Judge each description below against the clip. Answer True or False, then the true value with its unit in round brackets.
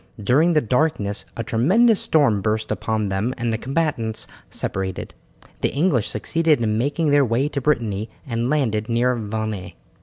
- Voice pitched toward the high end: False (120 Hz)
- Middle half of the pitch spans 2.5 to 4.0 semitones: False (5.2 semitones)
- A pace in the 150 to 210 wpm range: True (155 wpm)